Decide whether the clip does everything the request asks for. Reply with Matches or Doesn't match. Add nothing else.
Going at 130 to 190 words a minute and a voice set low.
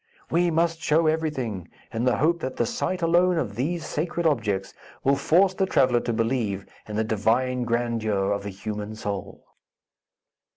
Matches